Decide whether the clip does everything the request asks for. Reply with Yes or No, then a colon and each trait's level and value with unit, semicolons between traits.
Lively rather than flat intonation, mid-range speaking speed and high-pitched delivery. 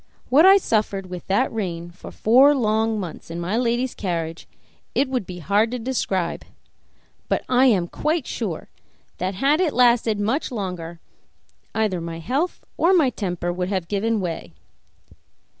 Yes: wide, 5.9 semitones; average, 160 wpm; high, 210 Hz